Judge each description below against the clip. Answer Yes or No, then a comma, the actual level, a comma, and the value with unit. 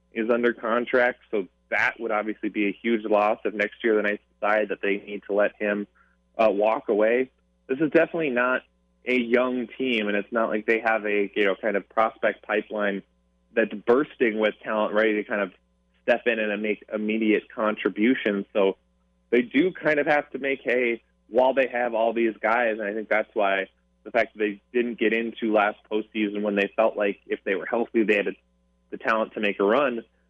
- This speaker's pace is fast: Yes, fast, 210 wpm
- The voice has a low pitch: Yes, low, 105 Hz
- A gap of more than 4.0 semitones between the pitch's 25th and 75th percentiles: No, average, 2.7 semitones